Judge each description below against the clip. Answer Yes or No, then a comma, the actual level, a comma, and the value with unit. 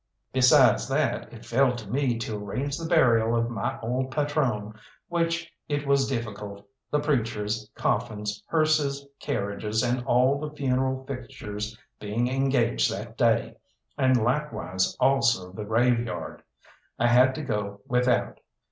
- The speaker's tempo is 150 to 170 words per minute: No, slow, 135 wpm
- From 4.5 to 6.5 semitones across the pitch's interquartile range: No, average, 4.0 semitones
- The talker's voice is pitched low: Yes, low, 120 Hz